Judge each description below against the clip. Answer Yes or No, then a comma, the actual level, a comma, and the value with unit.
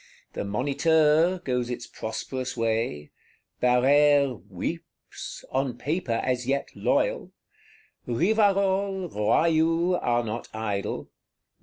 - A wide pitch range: Yes, wide, 5.7 semitones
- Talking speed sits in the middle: No, slow, 95 wpm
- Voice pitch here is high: No, low, 135 Hz